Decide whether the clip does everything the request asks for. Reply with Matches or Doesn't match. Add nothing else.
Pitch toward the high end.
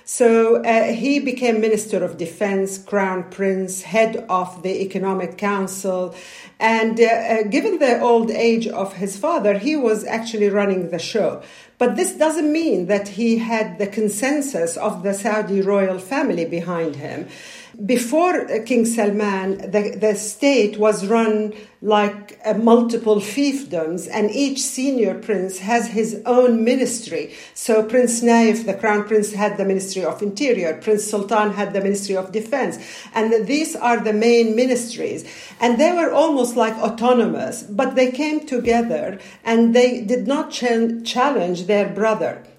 Matches